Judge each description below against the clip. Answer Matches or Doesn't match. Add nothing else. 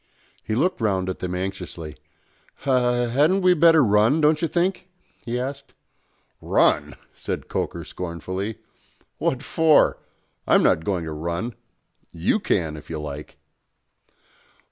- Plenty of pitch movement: Matches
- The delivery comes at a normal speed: Doesn't match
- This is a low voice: Matches